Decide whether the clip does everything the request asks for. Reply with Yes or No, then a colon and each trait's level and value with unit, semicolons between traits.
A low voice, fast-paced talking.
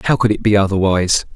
Yes: low, 100 Hz; fast, 220 wpm